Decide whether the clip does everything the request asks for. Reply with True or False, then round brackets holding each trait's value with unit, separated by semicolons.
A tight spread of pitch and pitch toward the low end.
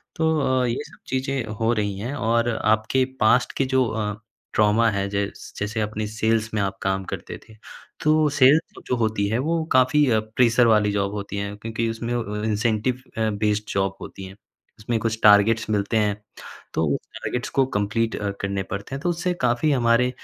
False (3.3 semitones; 110 Hz)